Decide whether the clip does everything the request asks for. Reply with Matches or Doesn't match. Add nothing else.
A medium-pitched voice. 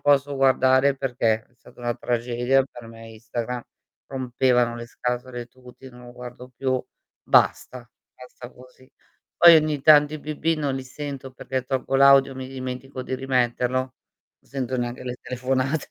Doesn't match